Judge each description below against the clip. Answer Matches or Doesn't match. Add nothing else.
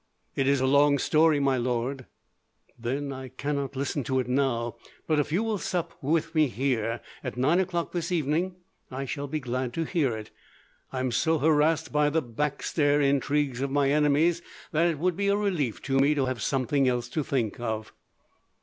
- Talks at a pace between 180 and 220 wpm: Matches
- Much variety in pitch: Doesn't match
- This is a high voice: Doesn't match